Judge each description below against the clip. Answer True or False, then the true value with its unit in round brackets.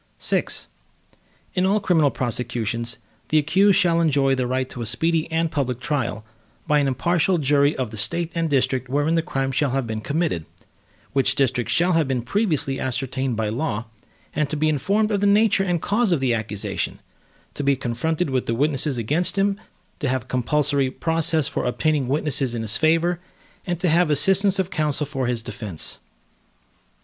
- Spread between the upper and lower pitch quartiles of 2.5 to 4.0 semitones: False (4.6 semitones)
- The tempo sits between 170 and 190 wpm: True (180 wpm)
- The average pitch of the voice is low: False (145 Hz)